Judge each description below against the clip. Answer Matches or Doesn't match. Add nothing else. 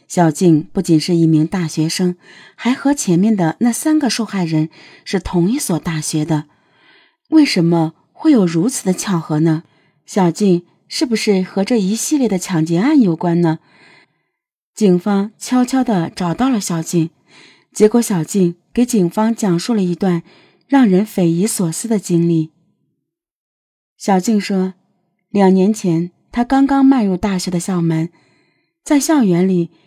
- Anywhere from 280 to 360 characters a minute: Doesn't match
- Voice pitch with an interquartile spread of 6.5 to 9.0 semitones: Doesn't match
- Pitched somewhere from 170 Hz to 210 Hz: Matches